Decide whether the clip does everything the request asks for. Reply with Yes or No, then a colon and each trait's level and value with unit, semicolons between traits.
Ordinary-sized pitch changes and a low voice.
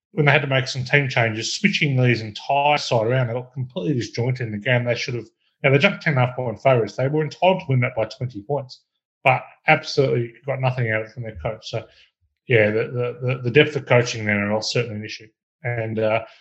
Yes: average, 3.7 semitones; low, 125 Hz